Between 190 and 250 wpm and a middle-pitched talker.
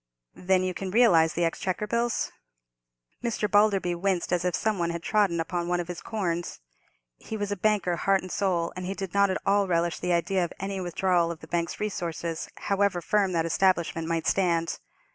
Yes: average, 200 wpm; medium, 180 Hz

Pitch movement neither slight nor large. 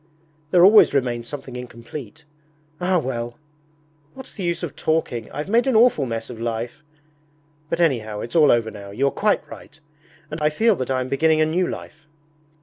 No: wide, 6.1 semitones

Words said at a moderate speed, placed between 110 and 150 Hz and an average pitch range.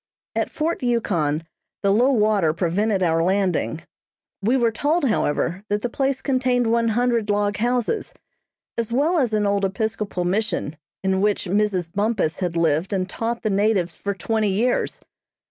No: average, 160 wpm; high, 210 Hz; average, 4.0 semitones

